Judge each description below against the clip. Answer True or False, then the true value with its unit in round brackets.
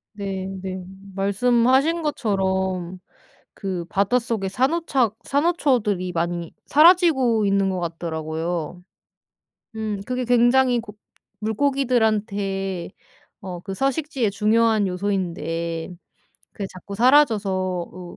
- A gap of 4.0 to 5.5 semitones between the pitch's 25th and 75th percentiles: True (5.1 semitones)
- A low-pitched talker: False (200 Hz)